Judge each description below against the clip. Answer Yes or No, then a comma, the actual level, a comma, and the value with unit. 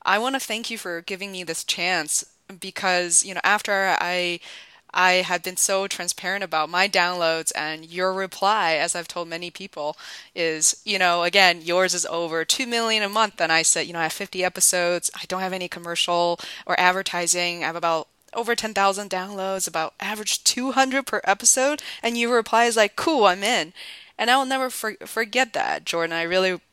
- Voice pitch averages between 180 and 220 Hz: Yes, medium, 185 Hz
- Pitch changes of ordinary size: Yes, average, 3.4 semitones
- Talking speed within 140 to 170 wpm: No, average, 195 wpm